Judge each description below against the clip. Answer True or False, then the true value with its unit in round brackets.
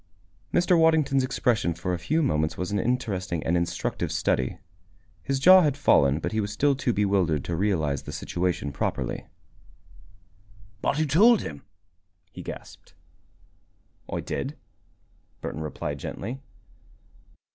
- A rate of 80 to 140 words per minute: True (135 wpm)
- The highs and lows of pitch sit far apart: True (8.9 semitones)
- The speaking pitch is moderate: False (100 Hz)